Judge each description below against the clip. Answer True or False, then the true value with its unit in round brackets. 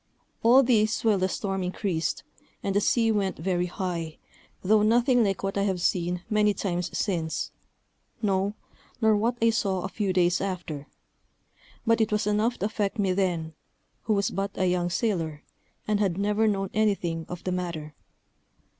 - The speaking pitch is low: False (195 Hz)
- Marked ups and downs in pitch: False (3.0 semitones)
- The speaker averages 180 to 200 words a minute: False (170 wpm)